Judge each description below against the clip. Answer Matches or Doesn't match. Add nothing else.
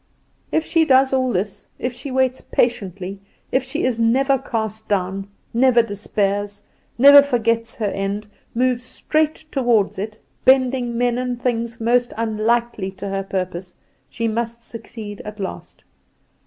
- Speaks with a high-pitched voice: Matches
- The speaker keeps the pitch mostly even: Doesn't match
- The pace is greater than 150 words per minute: Doesn't match